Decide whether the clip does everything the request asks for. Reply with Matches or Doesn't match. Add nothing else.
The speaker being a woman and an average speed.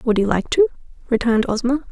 Matches